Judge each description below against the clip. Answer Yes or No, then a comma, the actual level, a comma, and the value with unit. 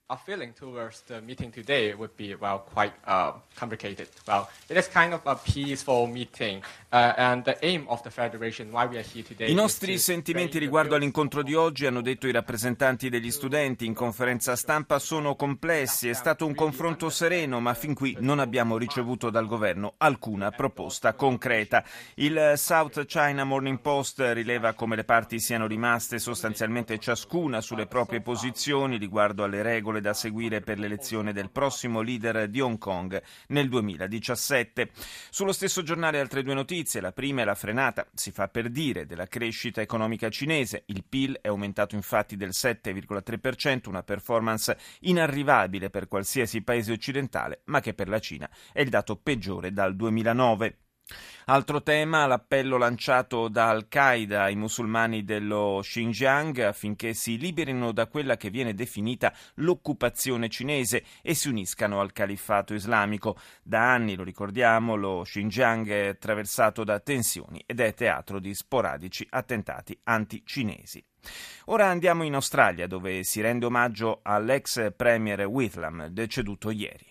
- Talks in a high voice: No, low, 120 Hz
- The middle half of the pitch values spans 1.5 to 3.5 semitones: No, average, 4.2 semitones